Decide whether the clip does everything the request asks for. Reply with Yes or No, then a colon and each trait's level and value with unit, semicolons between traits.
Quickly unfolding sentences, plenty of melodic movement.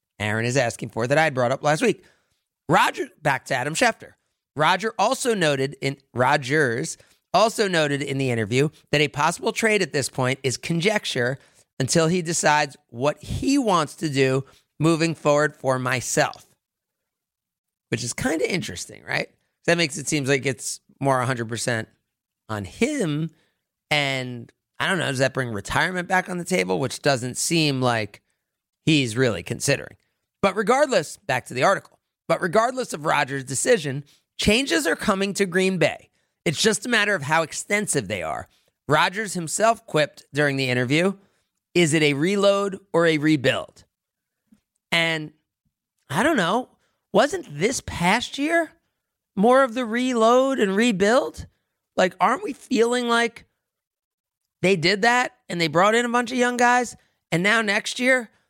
No: average, 160 wpm; wide, 7.6 semitones